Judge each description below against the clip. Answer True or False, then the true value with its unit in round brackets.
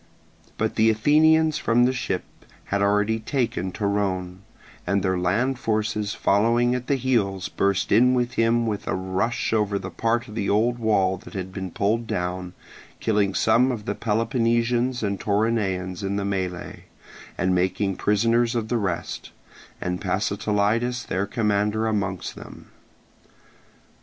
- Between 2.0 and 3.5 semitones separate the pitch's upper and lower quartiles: True (3.2 semitones)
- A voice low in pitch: True (105 Hz)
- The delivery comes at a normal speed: True (145 wpm)